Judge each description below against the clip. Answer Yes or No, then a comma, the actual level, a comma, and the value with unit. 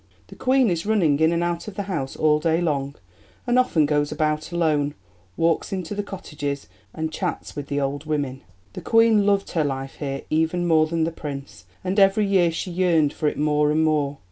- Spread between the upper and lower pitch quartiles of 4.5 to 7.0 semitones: No, average, 3.7 semitones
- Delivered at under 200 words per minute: No, fast, 205 wpm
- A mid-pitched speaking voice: Yes, medium, 160 Hz